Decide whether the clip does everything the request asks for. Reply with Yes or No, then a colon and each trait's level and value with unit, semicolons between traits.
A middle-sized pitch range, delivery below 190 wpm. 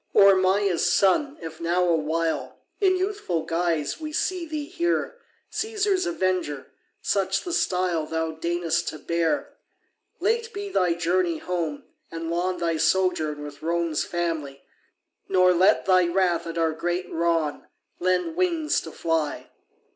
Yes: average, 4.0 semitones; average, 140 wpm